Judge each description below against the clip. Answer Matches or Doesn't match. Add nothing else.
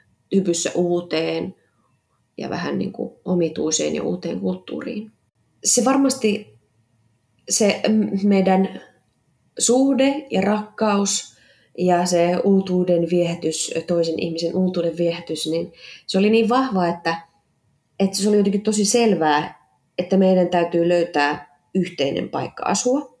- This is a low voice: Doesn't match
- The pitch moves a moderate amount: Matches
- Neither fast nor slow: Matches